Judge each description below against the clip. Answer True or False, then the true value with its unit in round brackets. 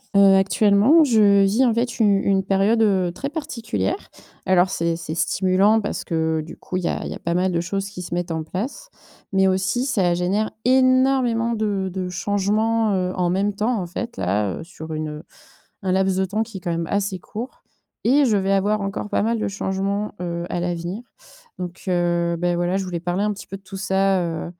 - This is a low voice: False (195 Hz)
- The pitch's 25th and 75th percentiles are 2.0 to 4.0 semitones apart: True (3.3 semitones)